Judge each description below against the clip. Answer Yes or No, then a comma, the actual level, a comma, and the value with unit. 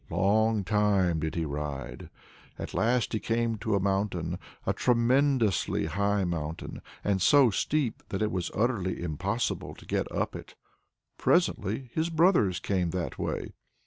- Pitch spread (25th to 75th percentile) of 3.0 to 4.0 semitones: No, average, 4.7 semitones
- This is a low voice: Yes, low, 100 Hz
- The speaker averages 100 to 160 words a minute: Yes, average, 145 wpm